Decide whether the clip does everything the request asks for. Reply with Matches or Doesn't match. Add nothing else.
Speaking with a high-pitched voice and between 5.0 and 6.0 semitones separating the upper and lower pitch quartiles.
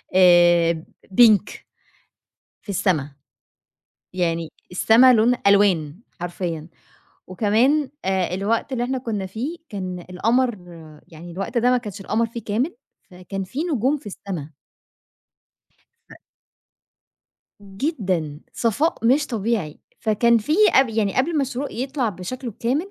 Matches